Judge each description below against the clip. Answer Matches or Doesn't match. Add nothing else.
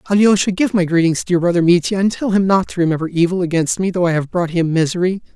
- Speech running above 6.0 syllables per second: Matches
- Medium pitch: Matches